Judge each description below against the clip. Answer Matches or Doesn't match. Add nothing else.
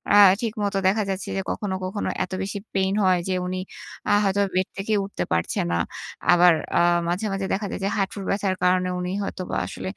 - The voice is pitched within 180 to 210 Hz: Matches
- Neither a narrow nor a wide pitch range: Doesn't match